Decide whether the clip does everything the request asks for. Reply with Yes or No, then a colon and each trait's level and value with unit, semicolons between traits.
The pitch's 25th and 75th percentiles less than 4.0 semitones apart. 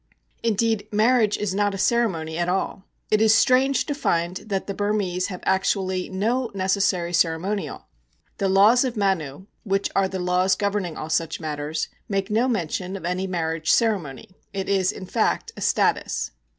Yes: average, 2.8 semitones